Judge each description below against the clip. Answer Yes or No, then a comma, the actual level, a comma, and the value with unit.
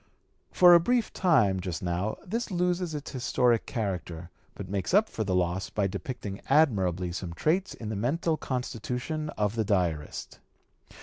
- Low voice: Yes, low, 110 Hz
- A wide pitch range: Yes, wide, 9.0 semitones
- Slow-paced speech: No, average, 160 wpm